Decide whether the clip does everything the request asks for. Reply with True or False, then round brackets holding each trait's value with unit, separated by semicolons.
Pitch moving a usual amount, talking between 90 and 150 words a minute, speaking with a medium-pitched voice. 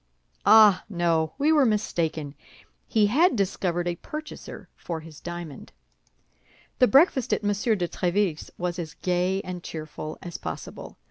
True (4.1 semitones; 140 wpm; 180 Hz)